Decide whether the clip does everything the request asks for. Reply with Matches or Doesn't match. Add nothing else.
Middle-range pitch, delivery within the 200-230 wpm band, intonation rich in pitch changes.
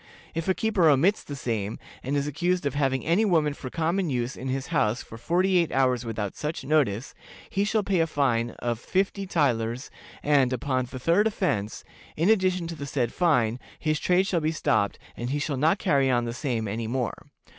Matches